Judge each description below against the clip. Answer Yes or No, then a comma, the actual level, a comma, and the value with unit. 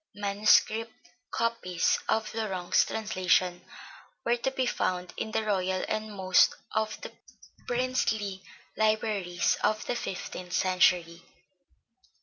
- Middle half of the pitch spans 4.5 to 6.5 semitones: No, average, 3.2 semitones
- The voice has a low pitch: No, high, 205 Hz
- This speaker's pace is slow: Yes, slow, 110 wpm